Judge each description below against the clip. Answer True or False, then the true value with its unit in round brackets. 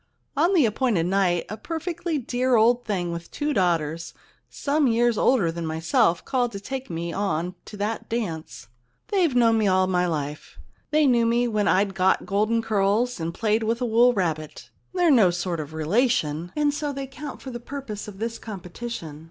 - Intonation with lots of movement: True (6.1 semitones)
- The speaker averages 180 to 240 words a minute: True (185 wpm)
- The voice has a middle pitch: False (215 Hz)